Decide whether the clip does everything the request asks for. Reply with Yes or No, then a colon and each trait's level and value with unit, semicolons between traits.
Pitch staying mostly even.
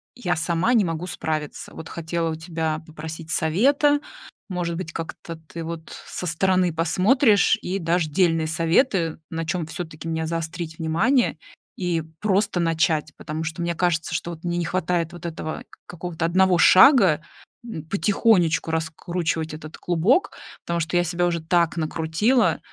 Yes: narrow, 2.1 semitones